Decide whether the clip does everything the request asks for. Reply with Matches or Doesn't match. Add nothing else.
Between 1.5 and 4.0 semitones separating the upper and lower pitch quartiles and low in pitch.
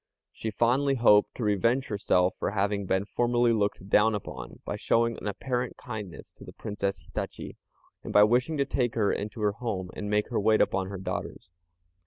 Matches